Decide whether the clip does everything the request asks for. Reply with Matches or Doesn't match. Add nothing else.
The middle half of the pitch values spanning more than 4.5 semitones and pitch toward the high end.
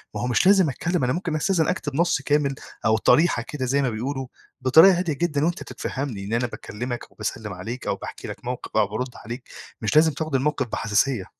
Doesn't match